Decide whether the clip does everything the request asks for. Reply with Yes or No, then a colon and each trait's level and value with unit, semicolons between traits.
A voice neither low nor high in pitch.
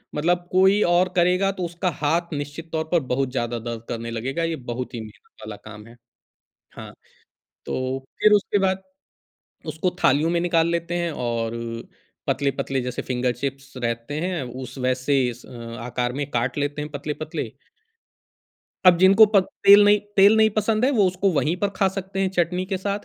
Yes: medium, 160 Hz